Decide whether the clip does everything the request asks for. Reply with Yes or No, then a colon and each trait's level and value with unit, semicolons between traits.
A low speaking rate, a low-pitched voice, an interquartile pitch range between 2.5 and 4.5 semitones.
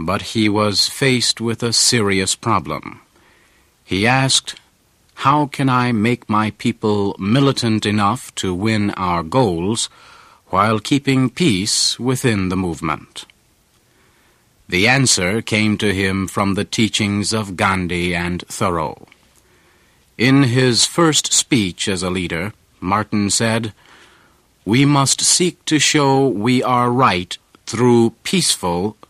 Yes: slow, 120 wpm; low, 110 Hz; average, 4.2 semitones